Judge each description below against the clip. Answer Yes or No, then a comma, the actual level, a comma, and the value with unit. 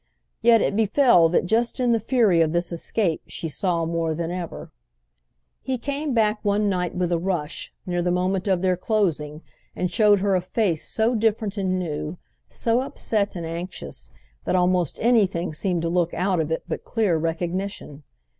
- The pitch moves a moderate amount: Yes, average, 4.0 semitones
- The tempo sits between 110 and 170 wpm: No, average, 180 wpm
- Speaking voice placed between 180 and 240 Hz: Yes, medium, 185 Hz